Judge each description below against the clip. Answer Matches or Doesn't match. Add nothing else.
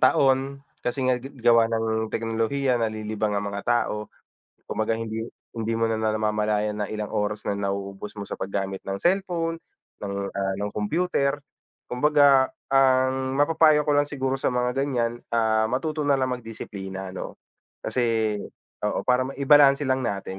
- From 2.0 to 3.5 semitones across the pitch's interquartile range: Doesn't match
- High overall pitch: Doesn't match